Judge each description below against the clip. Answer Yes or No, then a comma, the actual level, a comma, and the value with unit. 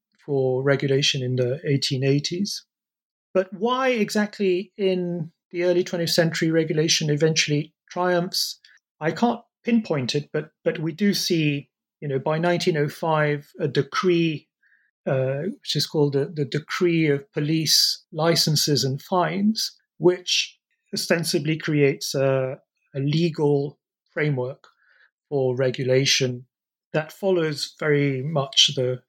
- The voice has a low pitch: No, medium, 155 Hz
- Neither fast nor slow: No, slow, 120 wpm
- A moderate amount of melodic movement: Yes, average, 4.1 semitones